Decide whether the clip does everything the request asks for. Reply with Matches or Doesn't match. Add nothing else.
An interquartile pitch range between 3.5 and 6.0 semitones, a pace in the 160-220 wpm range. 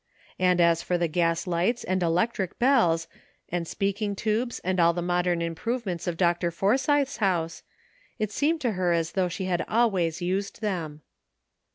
Matches